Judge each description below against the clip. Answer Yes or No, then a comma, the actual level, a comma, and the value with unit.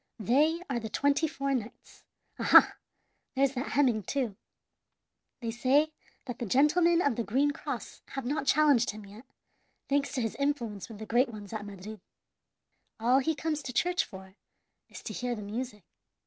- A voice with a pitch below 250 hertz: No, very high, 255 Hz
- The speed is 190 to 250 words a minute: No, average, 170 wpm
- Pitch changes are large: No, average, 4.7 semitones